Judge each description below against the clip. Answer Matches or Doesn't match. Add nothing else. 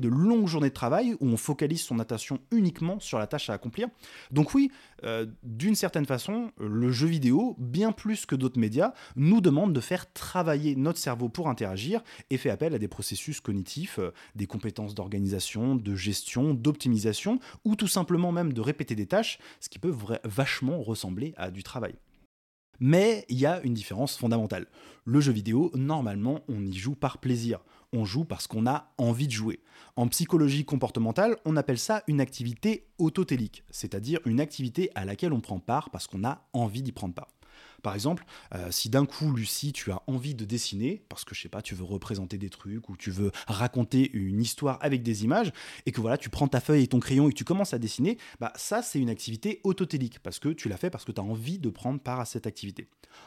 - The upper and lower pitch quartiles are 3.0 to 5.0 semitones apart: Doesn't match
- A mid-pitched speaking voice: Doesn't match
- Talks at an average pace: Matches